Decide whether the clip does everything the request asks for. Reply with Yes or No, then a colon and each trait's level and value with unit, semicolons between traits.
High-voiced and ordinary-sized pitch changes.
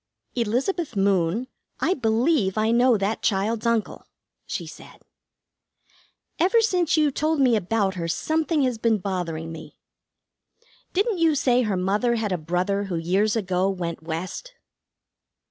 No: high, 220 Hz; wide, 5.9 semitones